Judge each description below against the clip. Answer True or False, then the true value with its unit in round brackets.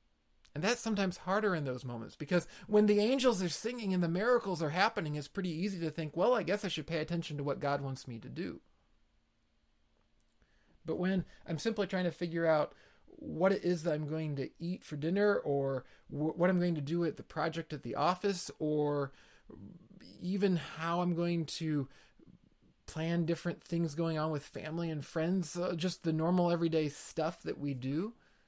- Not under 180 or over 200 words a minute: True (190 wpm)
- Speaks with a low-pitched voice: False (165 Hz)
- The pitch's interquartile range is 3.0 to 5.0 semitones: True (3.7 semitones)